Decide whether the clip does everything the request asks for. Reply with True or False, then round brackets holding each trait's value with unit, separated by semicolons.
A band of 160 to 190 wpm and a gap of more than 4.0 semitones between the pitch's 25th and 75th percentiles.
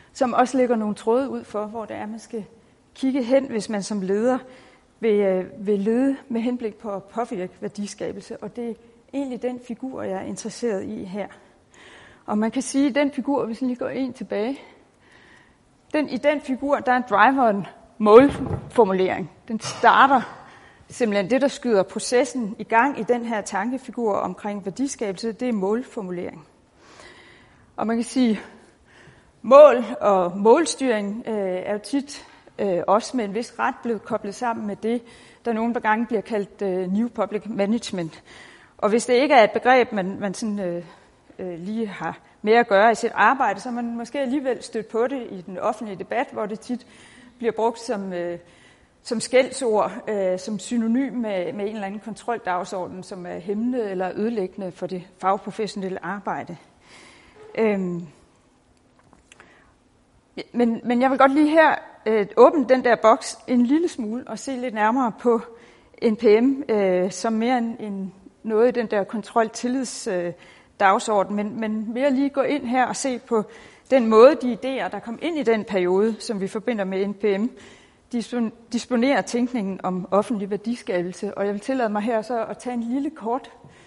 False (175 wpm; 3.4 semitones)